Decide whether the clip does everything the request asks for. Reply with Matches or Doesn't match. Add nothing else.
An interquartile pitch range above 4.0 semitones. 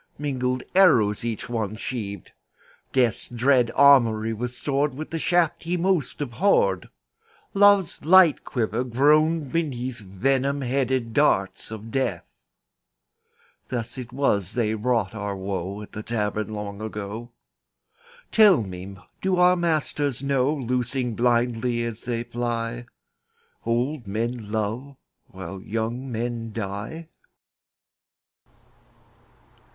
Matches